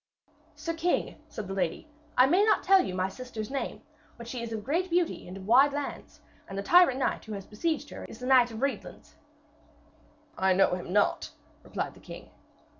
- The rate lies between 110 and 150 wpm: No, average, 200 wpm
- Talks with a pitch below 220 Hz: No, very high, 250 Hz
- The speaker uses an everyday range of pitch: No, wide, 7.2 semitones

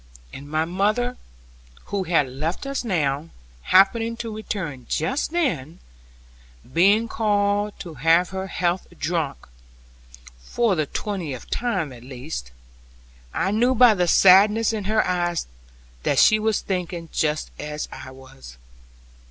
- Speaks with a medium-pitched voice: Yes, medium, 180 Hz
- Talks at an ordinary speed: No, slow, 130 wpm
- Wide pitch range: Yes, wide, 5.9 semitones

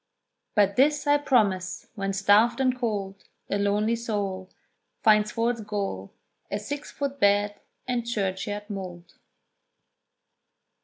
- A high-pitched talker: Yes, high, 210 Hz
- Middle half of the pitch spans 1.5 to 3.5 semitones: Yes, average, 3.2 semitones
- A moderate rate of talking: No, slow, 120 wpm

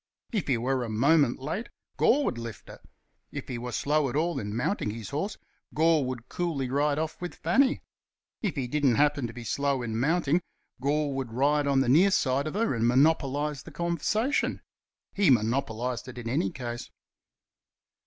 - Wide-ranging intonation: No, average, 4.6 semitones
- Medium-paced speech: Yes, average, 185 wpm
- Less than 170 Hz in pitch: Yes, medium, 140 Hz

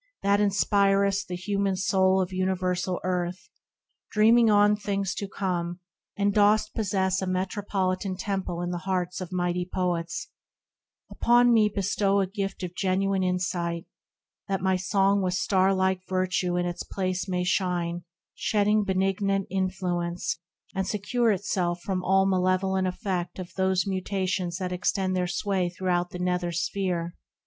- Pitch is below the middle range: No, high, 190 Hz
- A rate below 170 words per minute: Yes, average, 145 wpm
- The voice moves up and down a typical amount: No, narrow, 1.6 semitones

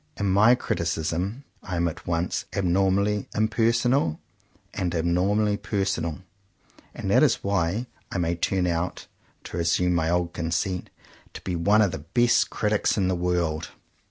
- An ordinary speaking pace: Yes, average, 155 wpm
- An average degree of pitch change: Yes, average, 3.2 semitones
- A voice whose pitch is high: No, very low, 90 Hz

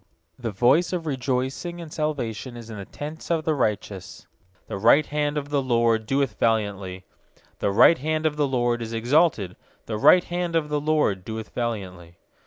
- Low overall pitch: Yes, low, 125 Hz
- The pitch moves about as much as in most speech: No, wide, 5.7 semitones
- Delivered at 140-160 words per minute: No, average, 180 wpm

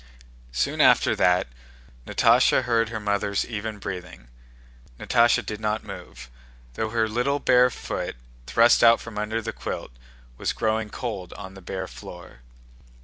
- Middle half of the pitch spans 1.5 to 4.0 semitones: Yes, average, 3.3 semitones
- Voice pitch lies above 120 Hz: No, low, 105 Hz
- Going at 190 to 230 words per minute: No, average, 145 wpm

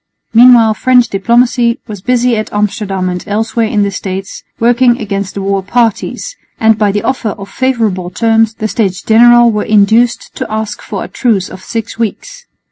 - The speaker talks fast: No, average, 175 wpm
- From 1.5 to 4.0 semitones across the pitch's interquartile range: Yes, average, 3.1 semitones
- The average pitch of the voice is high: Yes, high, 220 Hz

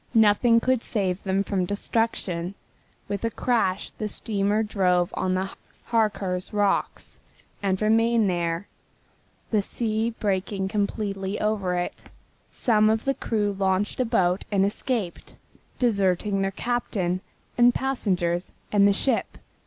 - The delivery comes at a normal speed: No, slow, 130 wpm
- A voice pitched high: Yes, high, 200 Hz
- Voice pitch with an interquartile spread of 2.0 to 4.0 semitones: Yes, average, 2.9 semitones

